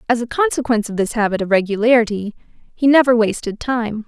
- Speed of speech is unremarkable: Yes, average, 175 wpm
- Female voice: Yes, female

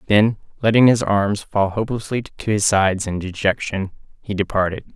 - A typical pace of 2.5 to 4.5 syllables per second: No, 5.1 syllables/s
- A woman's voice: No, male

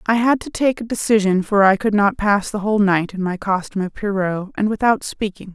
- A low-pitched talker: No, high, 205 Hz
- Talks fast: Yes, fast, 240 wpm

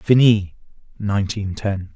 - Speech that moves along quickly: No, slow, 90 wpm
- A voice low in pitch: Yes, low, 100 Hz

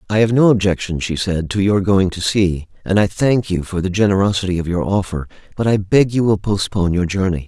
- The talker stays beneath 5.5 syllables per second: No, 5.7 syllables/s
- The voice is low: Yes, very low, 95 Hz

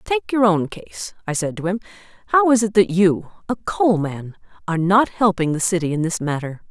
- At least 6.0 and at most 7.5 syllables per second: No, 5.1 syllables/s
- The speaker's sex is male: No, female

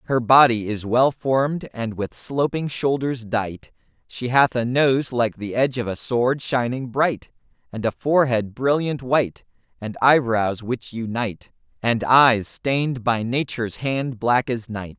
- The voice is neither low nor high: No, low, 120 Hz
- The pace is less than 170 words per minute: Yes, average, 160 wpm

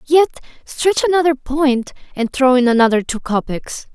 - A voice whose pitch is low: No, very high, 270 Hz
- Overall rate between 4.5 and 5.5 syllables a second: Yes, 4.9 syllables/s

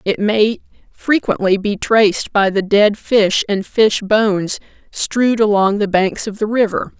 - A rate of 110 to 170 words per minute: Yes, average, 165 wpm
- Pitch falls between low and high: No, high, 210 Hz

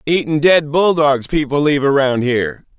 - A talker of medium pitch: Yes, medium, 145 Hz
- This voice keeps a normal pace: Yes, average, 150 wpm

